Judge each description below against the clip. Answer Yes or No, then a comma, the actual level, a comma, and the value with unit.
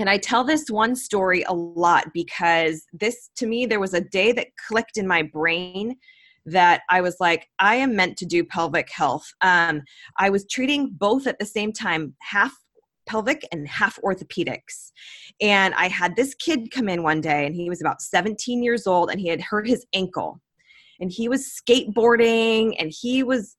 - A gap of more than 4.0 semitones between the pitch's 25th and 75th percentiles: Yes, wide, 5.5 semitones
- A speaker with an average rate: Yes, average, 190 wpm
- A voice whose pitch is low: No, high, 200 Hz